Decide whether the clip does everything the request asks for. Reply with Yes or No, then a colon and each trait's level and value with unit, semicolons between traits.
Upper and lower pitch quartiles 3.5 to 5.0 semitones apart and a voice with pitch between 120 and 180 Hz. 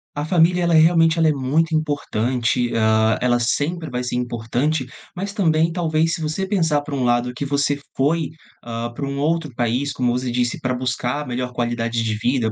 Yes: average, 4.7 semitones; low, 135 Hz